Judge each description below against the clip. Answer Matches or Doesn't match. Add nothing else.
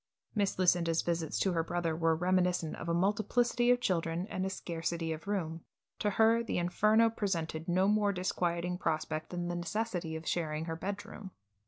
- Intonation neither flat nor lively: Matches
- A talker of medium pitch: Matches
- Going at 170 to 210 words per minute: Matches